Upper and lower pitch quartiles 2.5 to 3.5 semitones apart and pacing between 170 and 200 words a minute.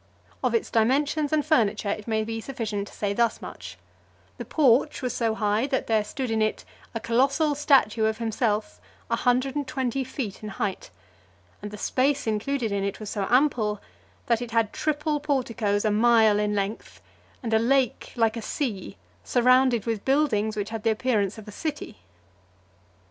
No: average, 3.9 semitones; average, 180 wpm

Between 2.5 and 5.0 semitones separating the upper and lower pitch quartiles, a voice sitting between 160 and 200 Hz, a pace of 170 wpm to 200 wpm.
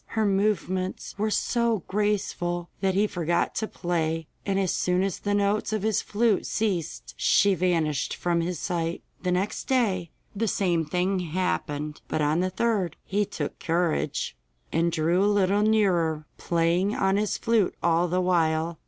No: average, 3.3 semitones; medium, 185 Hz; average, 160 wpm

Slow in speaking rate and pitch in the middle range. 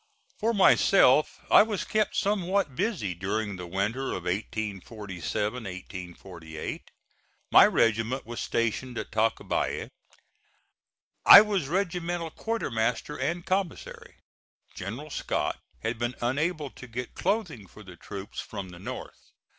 No: slow, 120 wpm; low, 120 Hz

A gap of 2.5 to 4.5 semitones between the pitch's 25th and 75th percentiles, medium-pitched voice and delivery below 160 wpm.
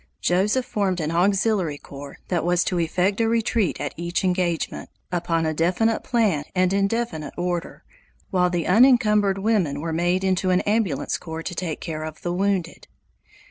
No: average, 3.3 semitones; medium, 180 Hz; average, 170 wpm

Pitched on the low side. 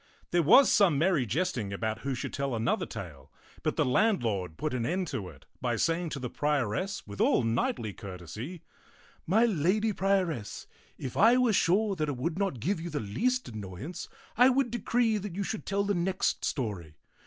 No: medium, 160 Hz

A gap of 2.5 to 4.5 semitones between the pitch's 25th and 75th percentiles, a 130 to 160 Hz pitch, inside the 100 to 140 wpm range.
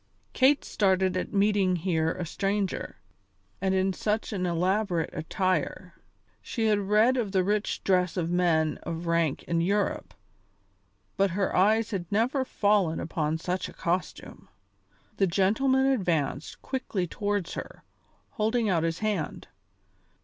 No: average, 3.5 semitones; high, 190 Hz; slow, 135 wpm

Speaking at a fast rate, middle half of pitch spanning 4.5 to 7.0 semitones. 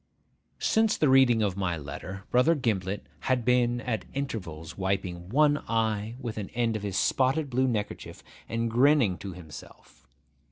No: average, 155 wpm; average, 5.1 semitones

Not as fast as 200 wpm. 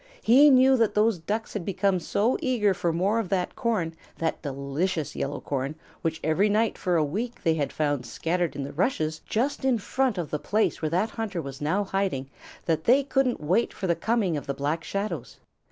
No: fast, 205 wpm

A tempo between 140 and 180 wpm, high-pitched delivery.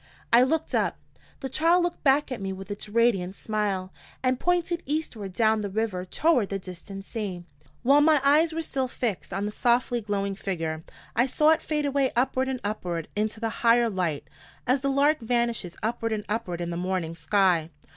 No: average, 190 wpm; high, 225 Hz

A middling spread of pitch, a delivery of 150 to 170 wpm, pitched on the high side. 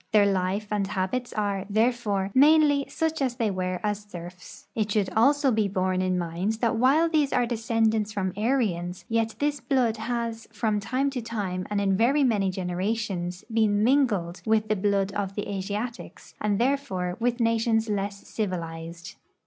Yes: average, 3.7 semitones; average, 165 wpm; high, 215 Hz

